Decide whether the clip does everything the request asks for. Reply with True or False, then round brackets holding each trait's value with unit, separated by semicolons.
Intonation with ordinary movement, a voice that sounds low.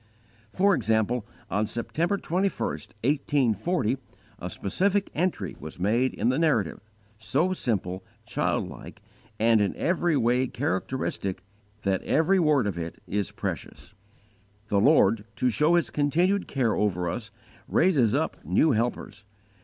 False (7.6 semitones; 120 Hz)